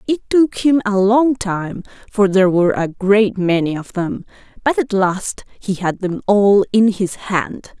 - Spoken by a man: No, female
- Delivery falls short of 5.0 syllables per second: Yes, 4.0 syllables/s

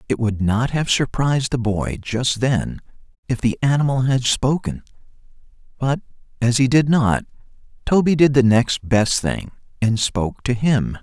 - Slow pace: No, average, 160 wpm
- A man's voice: Yes, male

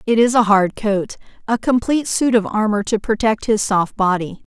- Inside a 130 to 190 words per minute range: No, average, 200 wpm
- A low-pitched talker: No, high, 215 Hz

